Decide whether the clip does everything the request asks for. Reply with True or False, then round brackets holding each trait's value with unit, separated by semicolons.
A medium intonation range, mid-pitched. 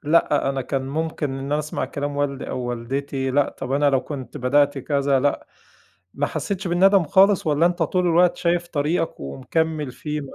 True (3.3 semitones; 145 Hz)